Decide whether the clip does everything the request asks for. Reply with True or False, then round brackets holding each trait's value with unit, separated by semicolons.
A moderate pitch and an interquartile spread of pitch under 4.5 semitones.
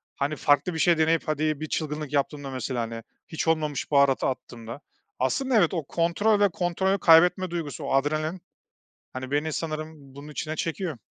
True (155 Hz; 3.1 semitones)